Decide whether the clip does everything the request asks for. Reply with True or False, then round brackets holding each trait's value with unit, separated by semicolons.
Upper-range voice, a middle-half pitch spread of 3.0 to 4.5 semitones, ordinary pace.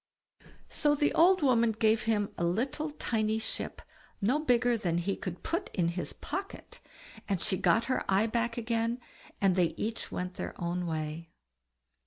False (220 Hz; 5.2 semitones; 160 wpm)